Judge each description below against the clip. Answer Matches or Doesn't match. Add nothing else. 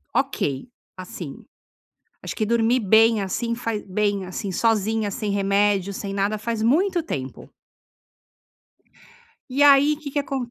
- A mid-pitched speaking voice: Doesn't match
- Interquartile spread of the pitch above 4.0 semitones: Doesn't match